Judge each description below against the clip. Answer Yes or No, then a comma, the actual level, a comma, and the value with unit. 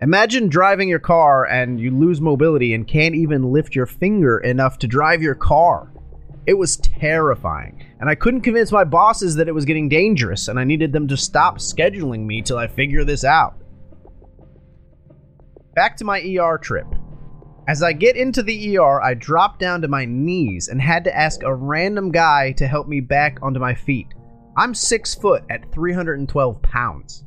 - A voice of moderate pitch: Yes, medium, 150 Hz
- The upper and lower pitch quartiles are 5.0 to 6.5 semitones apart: Yes, average, 5.3 semitones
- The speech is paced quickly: No, average, 185 wpm